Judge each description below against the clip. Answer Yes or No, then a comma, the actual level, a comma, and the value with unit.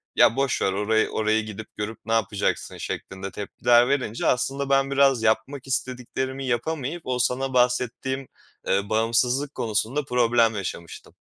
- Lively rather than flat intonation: No, average, 3.4 semitones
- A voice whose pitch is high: No, low, 120 Hz